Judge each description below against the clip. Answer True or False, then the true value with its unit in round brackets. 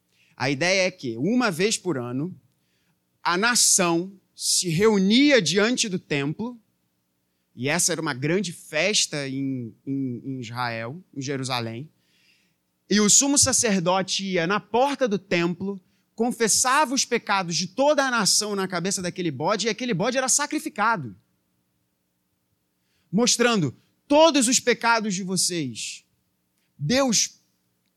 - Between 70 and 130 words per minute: True (125 wpm)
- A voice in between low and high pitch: True (180 Hz)